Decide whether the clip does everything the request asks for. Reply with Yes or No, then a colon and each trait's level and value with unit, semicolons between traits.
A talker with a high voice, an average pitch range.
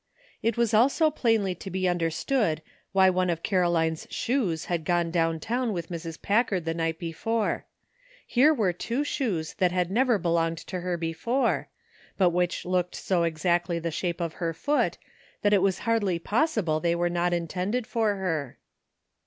No: medium, 180 Hz; average, 4.5 semitones